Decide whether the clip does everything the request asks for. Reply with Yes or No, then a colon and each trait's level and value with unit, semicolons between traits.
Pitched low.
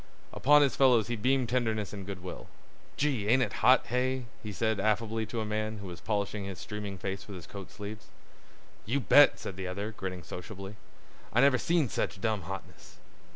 Yes: low, 105 Hz